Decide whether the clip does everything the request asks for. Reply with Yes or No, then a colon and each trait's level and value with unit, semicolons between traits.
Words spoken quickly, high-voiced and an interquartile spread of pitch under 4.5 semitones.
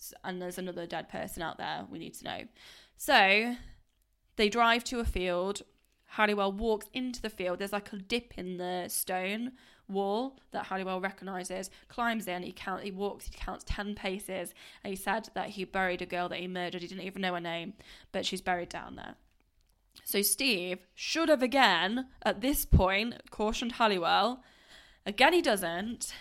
No: average, 180 wpm; high, 195 Hz; average, 3.6 semitones